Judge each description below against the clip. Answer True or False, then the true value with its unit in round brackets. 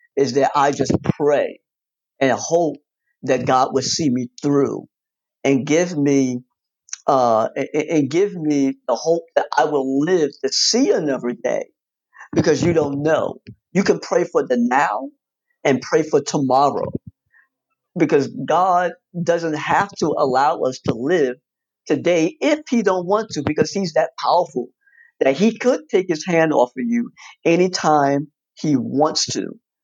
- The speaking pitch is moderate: True (165 Hz)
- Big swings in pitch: True (7.1 semitones)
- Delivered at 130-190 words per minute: True (155 wpm)